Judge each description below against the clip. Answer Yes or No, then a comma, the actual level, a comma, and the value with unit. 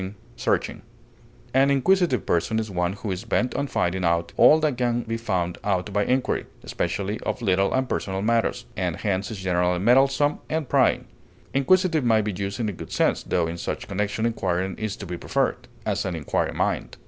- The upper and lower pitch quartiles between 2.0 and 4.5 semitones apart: No, average, 5.2 semitones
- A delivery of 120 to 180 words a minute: No, average, 190 wpm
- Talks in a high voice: No, low, 105 Hz